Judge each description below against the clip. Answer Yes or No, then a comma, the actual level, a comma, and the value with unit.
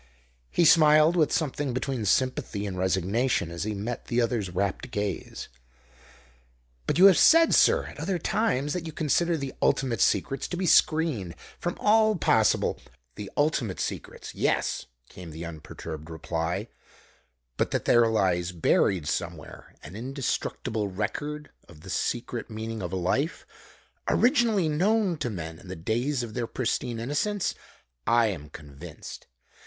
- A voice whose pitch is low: Yes, low, 115 Hz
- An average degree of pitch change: No, wide, 8.3 semitones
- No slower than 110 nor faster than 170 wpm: Yes, average, 150 wpm